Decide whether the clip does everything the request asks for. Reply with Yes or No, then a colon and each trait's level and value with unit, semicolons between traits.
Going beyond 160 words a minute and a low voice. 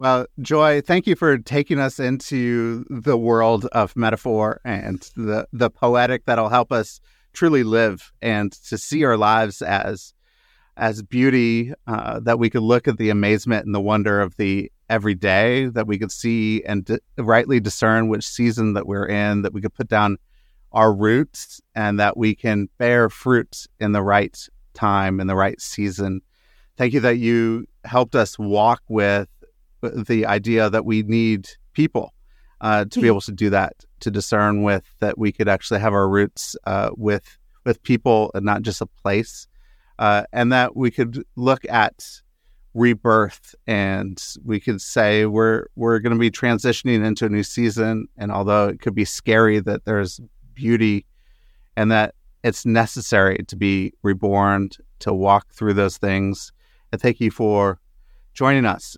Yes: average, 170 wpm; low, 110 Hz